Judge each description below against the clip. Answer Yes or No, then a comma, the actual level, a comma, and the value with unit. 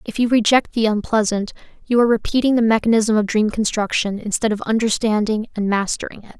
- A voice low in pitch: No, high, 220 Hz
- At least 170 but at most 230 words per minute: Yes, average, 180 wpm